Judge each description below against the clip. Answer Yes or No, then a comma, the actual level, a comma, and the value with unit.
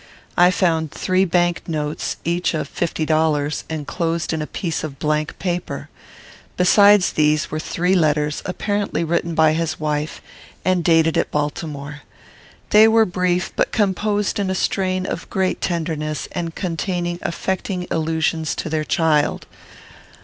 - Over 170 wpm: No, average, 140 wpm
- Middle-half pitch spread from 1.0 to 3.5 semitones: Yes, average, 2.9 semitones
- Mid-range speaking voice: Yes, medium, 165 Hz